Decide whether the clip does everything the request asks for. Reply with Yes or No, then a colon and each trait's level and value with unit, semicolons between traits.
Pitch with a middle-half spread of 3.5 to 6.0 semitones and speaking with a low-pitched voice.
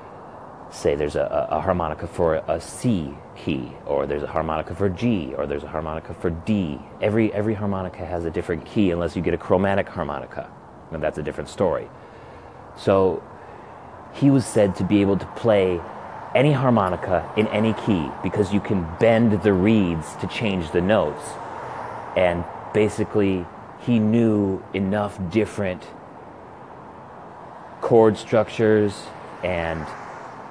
Yes: average, 3.8 semitones; very low, 95 Hz